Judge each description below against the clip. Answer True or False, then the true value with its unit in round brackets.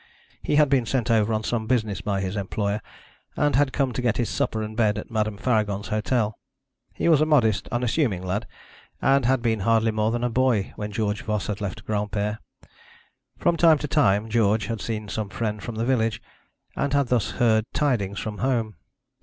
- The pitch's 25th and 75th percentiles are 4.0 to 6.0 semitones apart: False (3.1 semitones)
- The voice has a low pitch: True (110 Hz)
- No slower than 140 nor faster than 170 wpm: False (195 wpm)